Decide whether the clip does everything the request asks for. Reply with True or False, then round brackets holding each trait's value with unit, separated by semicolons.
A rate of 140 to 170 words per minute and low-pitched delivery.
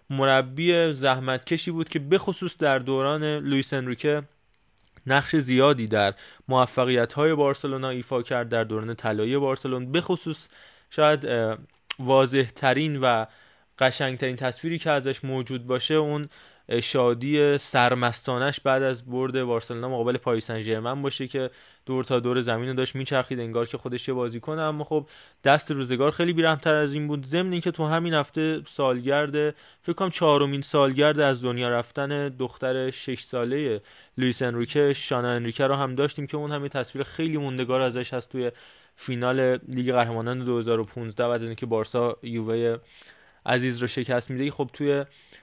True (150 wpm; 130 Hz)